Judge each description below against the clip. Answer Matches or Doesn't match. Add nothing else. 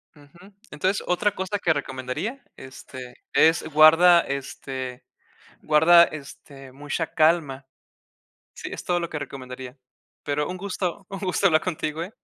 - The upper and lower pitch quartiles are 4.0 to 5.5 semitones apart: Matches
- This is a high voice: Doesn't match